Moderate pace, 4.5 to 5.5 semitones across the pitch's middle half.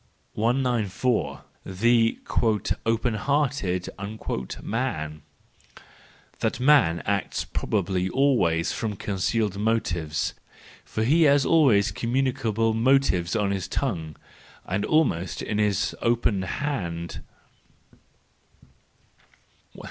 No: slow, 90 wpm; average, 5.2 semitones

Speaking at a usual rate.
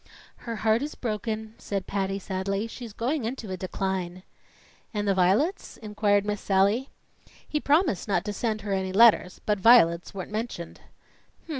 Yes: average, 155 wpm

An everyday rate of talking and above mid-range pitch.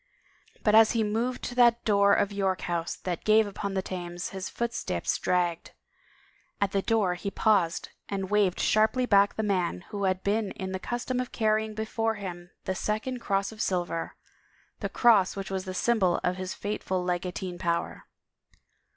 Yes: average, 175 wpm; high, 200 Hz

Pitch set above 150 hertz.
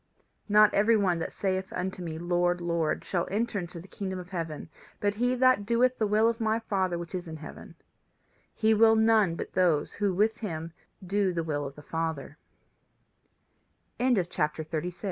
Yes: medium, 185 Hz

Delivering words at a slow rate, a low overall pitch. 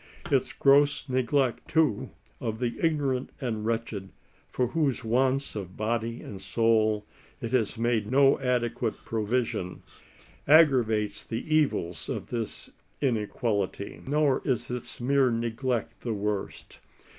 Yes: slow, 120 wpm; low, 120 Hz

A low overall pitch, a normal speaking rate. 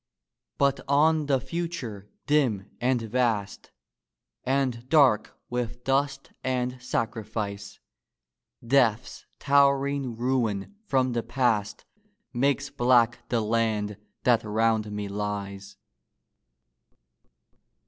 No: low, 120 Hz; slow, 90 wpm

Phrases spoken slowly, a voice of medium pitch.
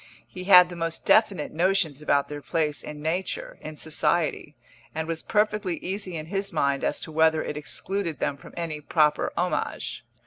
No: average, 175 wpm; medium, 160 Hz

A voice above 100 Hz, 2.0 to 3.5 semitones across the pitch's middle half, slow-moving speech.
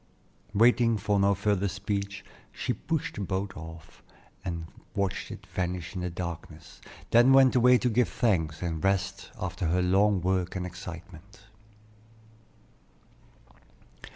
No: very low, 95 Hz; average, 2.7 semitones; slow, 130 wpm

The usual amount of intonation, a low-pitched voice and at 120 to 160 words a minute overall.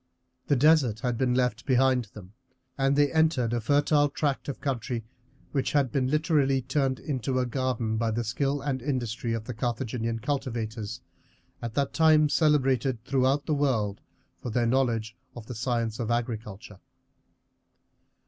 Yes: average, 3.3 semitones; low, 125 Hz; average, 155 wpm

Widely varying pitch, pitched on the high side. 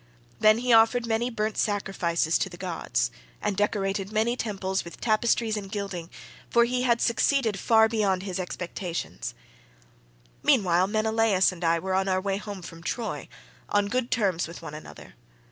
No: average, 3.5 semitones; high, 200 Hz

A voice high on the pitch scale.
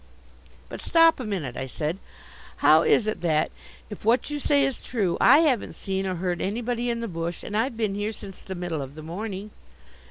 Yes: high, 205 Hz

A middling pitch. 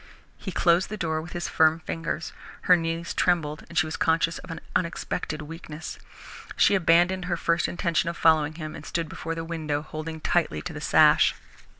Yes: medium, 165 Hz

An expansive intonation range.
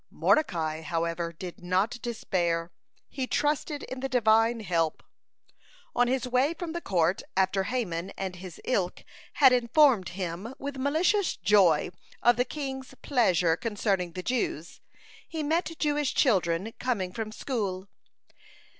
Yes: wide, 6.6 semitones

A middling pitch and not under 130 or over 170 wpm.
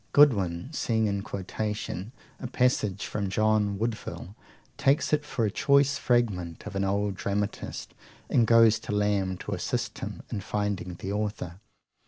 No: low, 105 Hz; average, 150 wpm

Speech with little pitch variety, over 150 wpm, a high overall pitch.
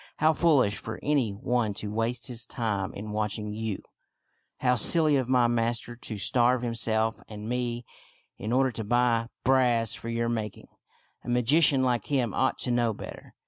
No: narrow, 2.2 semitones; average, 175 wpm; low, 120 Hz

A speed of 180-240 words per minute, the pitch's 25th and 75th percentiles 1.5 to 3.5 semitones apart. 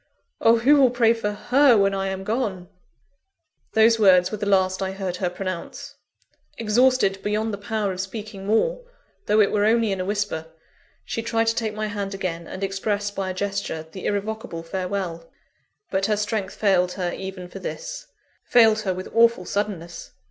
Yes: average, 185 wpm; average, 2.7 semitones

